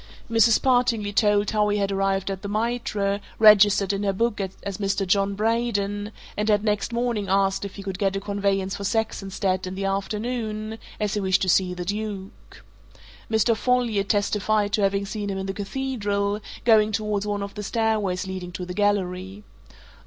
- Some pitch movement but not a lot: No, narrow, 1.7 semitones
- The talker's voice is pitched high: Yes, high, 205 Hz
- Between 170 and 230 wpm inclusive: Yes, average, 180 wpm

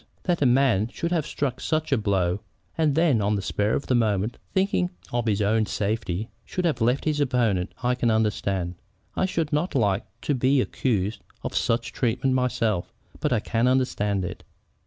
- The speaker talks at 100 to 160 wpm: No, average, 185 wpm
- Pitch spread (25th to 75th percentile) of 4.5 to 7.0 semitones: Yes, average, 5.1 semitones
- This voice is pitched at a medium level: No, low, 120 Hz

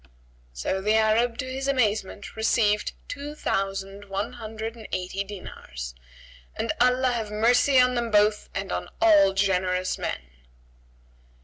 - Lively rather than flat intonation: No, average, 3.5 semitones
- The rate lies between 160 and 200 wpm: No, slow, 135 wpm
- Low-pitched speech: No, high, 215 Hz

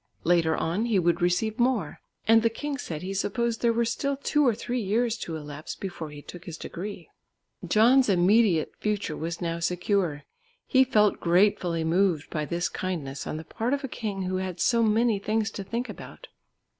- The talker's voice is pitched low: No, high, 195 Hz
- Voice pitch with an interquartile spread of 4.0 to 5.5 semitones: Yes, average, 5.1 semitones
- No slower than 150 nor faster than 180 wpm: No, average, 190 wpm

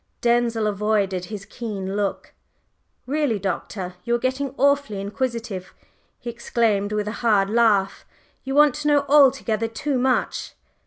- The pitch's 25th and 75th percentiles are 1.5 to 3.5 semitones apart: No, average, 4.3 semitones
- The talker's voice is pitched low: No, high, 230 Hz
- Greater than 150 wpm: No, average, 140 wpm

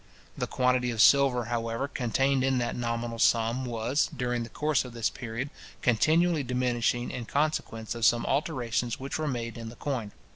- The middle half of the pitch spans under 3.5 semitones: Yes, narrow, 2.5 semitones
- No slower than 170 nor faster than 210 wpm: Yes, average, 175 wpm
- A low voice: Yes, low, 120 Hz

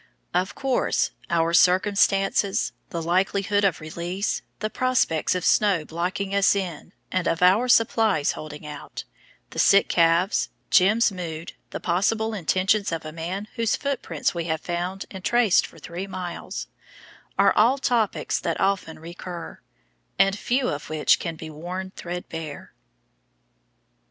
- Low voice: No, medium, 185 Hz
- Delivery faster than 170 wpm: No, average, 140 wpm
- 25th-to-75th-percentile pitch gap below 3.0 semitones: No, average, 3.3 semitones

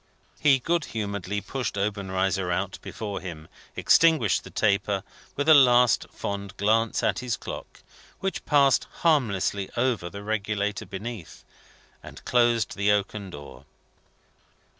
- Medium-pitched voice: No, low, 105 Hz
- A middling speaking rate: No, slow, 125 wpm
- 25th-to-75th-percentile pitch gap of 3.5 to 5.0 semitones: Yes, average, 3.8 semitones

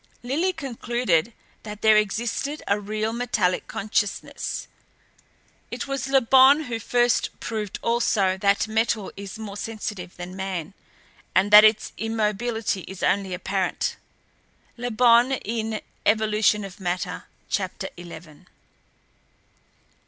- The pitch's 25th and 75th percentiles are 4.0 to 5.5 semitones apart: No, average, 3.4 semitones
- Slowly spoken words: Yes, slow, 115 wpm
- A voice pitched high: Yes, high, 215 Hz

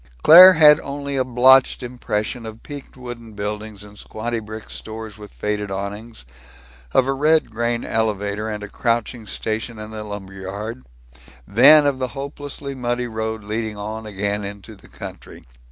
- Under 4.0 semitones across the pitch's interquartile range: Yes, average, 3.5 semitones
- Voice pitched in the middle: No, low, 110 Hz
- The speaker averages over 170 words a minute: No, average, 155 wpm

